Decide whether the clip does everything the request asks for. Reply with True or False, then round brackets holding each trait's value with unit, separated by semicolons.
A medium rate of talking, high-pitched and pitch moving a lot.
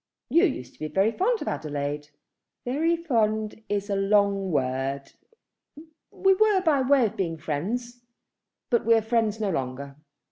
True (155 wpm; 210 Hz; 8.3 semitones)